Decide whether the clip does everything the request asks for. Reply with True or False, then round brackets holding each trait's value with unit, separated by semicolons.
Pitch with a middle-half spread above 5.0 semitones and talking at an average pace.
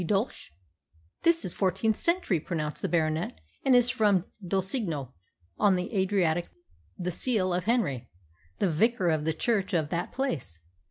True (5.4 semitones; 160 wpm)